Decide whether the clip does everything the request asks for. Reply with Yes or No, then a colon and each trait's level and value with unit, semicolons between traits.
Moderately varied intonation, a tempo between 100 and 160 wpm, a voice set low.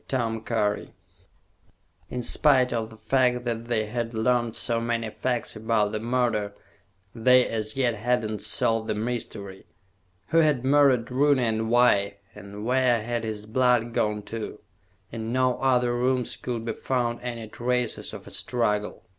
No: narrow, 2.2 semitones; average, 150 wpm; low, 120 Hz